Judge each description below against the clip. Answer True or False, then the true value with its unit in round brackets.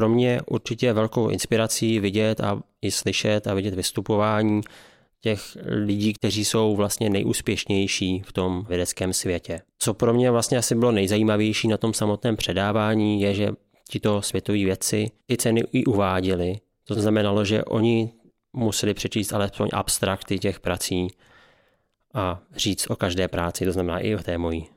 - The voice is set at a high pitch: False (105 Hz)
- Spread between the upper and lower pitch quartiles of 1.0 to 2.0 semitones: False (2.6 semitones)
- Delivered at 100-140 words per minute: False (155 wpm)